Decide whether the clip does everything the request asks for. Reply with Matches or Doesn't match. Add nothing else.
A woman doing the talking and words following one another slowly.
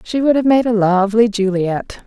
Doesn't match